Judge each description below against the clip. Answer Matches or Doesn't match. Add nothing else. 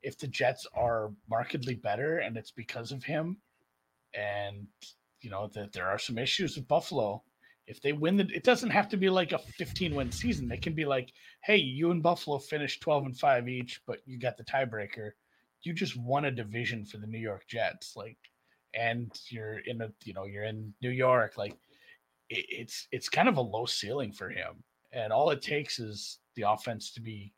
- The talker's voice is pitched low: Matches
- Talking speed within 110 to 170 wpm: Doesn't match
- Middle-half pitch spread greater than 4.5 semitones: Matches